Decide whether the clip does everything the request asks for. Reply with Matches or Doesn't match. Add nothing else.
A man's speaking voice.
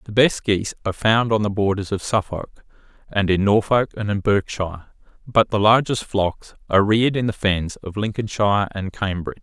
Matches